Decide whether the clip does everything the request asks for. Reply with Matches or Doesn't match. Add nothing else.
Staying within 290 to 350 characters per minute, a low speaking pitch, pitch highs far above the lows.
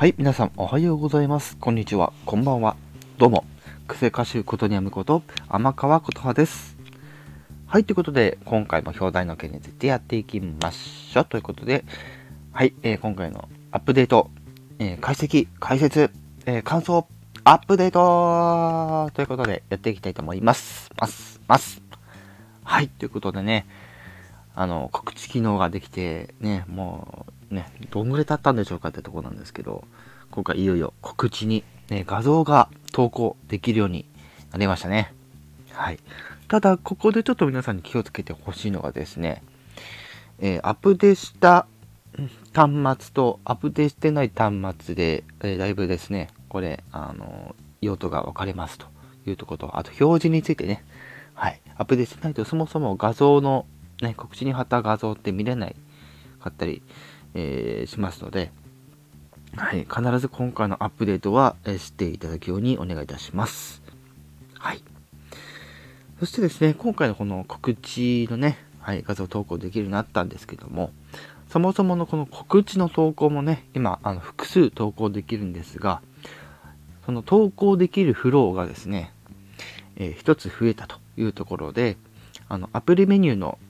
Matches